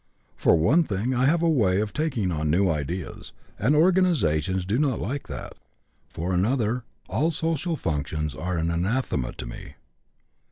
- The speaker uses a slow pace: No, average, 155 wpm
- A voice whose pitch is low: Yes, low, 105 Hz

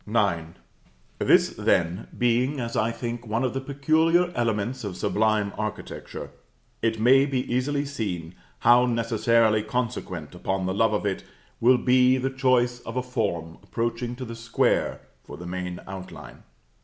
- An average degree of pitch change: Yes, average, 3.7 semitones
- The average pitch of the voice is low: Yes, low, 115 Hz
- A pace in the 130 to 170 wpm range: Yes, average, 155 wpm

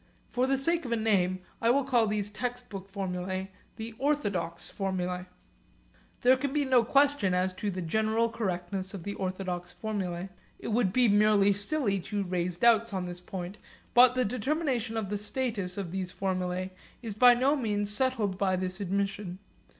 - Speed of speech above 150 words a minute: Yes, average, 175 wpm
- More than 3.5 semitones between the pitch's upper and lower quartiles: Yes, average, 4.4 semitones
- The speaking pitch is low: No, high, 205 Hz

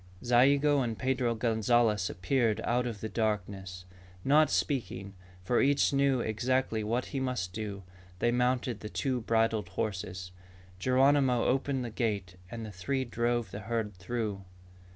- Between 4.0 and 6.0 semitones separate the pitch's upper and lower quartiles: No, average, 3.5 semitones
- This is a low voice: Yes, low, 115 Hz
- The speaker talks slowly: No, average, 145 wpm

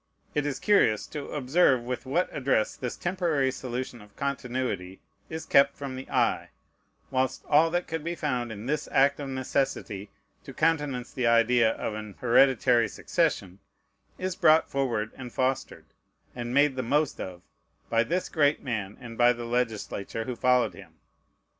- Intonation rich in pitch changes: No, average, 3.7 semitones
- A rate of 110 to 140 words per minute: No, average, 160 wpm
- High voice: No, low, 130 Hz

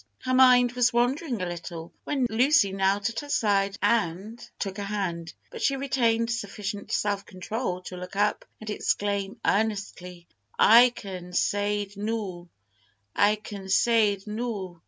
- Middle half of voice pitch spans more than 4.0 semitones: No, average, 3.3 semitones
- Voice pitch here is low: No, high, 205 Hz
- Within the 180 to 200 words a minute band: No, average, 145 wpm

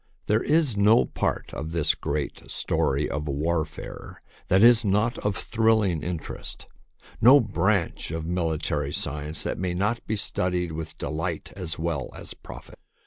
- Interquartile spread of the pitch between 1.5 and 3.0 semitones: No, average, 5.1 semitones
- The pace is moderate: Yes, average, 150 wpm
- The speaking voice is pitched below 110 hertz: Yes, very low, 85 Hz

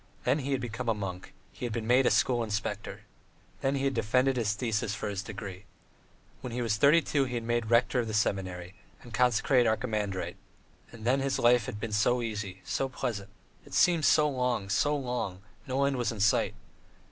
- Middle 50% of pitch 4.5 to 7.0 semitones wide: No, average, 3.4 semitones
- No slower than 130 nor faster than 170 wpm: No, fast, 205 wpm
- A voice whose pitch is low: Yes, low, 120 Hz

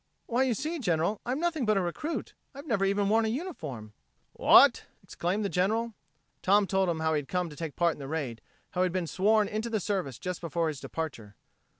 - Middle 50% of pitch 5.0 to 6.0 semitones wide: Yes, wide, 5.4 semitones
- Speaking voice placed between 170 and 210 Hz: Yes, high, 190 Hz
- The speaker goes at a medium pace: No, fast, 225 wpm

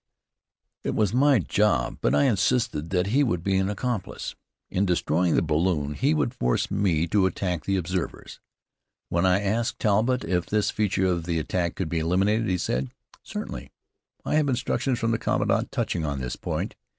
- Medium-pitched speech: No, very low, 95 Hz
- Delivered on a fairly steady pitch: No, average, 4.7 semitones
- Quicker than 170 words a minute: Yes, average, 180 wpm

